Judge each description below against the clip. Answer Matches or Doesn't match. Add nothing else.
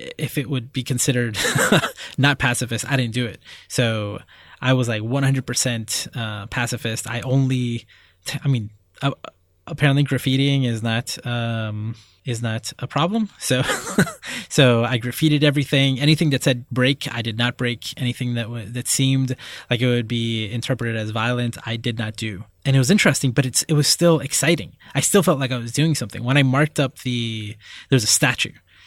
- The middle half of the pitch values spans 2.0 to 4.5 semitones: Matches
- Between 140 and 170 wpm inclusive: Doesn't match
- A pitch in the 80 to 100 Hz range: Doesn't match